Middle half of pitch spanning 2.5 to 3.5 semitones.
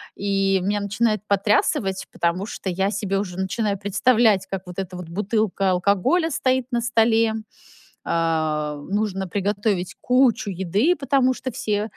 Yes: average, 3.1 semitones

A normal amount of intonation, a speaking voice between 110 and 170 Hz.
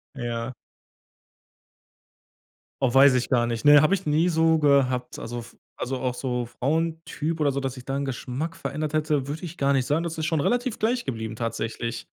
Yes: average, 4.2 semitones; medium, 140 Hz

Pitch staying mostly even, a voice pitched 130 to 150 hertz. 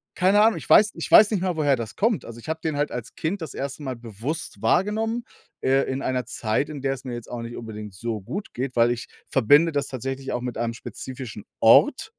No: wide, 5.4 semitones; low, 135 Hz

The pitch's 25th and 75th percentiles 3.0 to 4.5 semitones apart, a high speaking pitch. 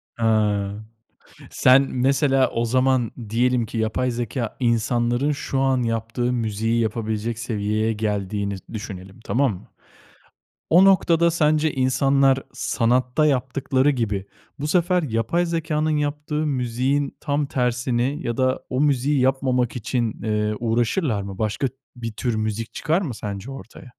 No: average, 3.7 semitones; low, 125 Hz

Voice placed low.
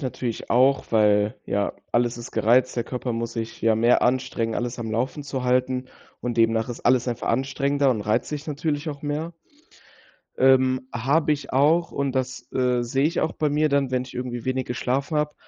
Yes: low, 130 Hz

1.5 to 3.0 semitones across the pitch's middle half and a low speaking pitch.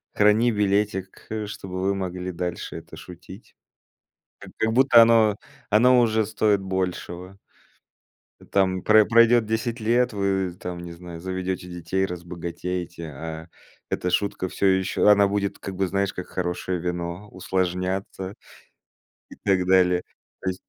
Yes: narrow, 2.6 semitones; very low, 95 Hz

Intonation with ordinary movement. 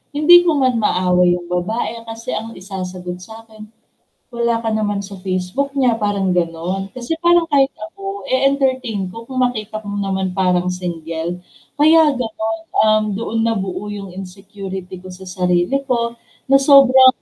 No: wide, 5.8 semitones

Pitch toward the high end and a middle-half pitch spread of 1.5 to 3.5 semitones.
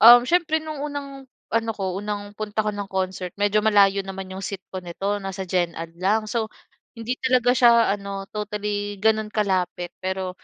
Yes: high, 205 Hz; average, 2.9 semitones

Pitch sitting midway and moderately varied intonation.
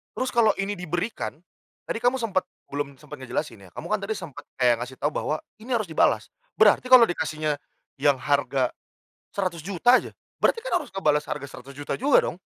No: medium, 170 Hz; wide, 7.5 semitones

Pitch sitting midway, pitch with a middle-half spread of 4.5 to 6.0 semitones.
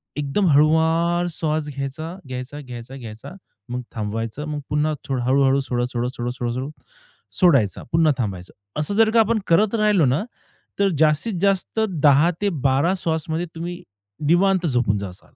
Yes: medium, 150 Hz; wide, 5.4 semitones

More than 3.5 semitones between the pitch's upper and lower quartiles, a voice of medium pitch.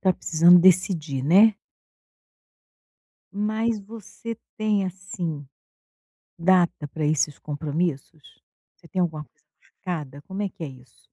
Yes: average, 4.4 semitones; medium, 175 Hz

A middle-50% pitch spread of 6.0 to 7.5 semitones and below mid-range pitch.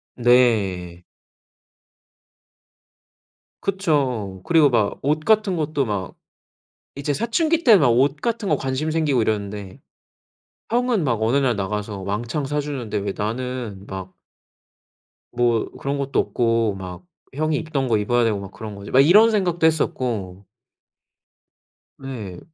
Yes: wide, 6.7 semitones; low, 125 Hz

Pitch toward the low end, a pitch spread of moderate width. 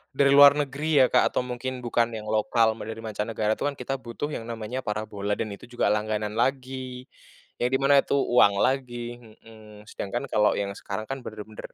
Yes: low, 120 Hz; average, 3.3 semitones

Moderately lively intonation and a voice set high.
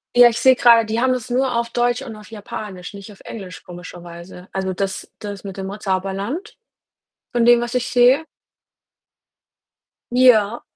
Yes: average, 4.0 semitones; high, 220 Hz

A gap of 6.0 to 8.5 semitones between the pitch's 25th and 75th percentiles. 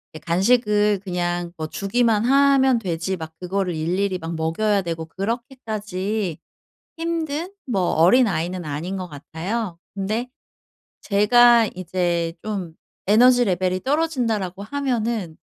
No: average, 5.2 semitones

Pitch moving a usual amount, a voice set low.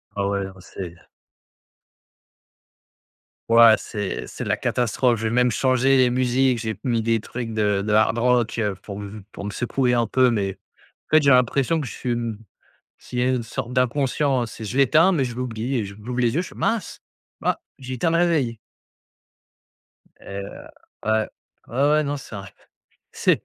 Yes: average, 3.0 semitones; low, 120 Hz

